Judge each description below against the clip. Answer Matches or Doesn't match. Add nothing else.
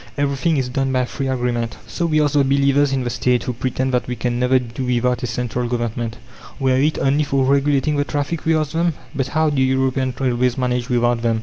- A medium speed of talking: Doesn't match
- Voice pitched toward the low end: Matches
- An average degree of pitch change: Doesn't match